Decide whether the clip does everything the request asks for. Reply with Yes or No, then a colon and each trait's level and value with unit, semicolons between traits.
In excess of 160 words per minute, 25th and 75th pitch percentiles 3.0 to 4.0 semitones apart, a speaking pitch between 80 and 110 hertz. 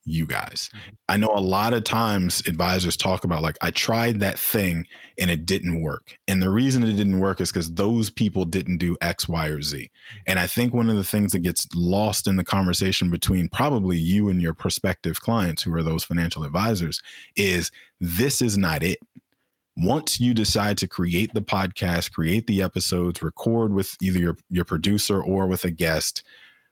Yes: average, 195 wpm; average, 3.3 semitones; very low, 95 Hz